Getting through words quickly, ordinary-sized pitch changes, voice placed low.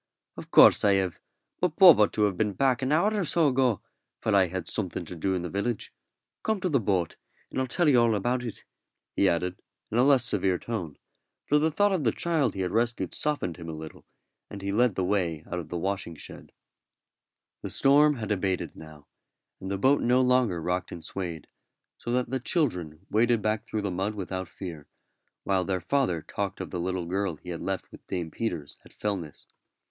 No: fast, 215 wpm; wide, 5.9 semitones; low, 100 Hz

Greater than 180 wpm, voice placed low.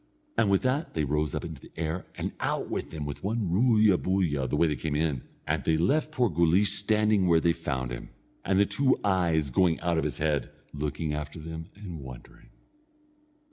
Yes: average, 200 wpm; very low, 85 Hz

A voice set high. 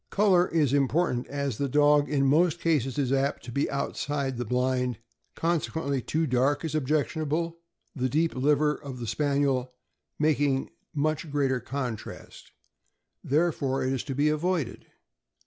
No: medium, 140 Hz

